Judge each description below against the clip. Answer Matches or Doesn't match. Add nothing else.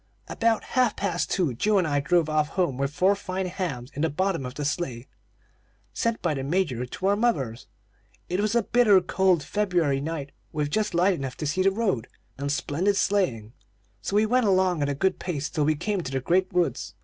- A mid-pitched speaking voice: Matches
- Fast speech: Matches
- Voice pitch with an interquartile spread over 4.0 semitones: Matches